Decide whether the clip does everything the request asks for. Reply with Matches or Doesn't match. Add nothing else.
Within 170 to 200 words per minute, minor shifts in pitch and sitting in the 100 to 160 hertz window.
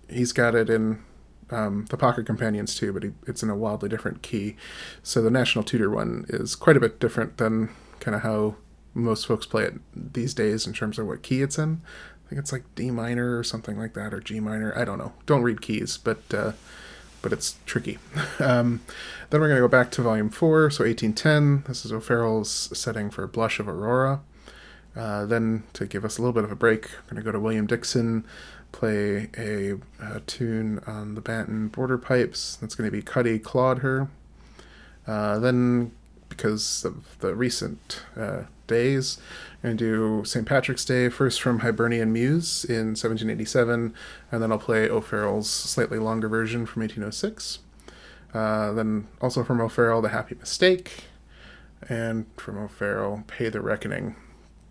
Matches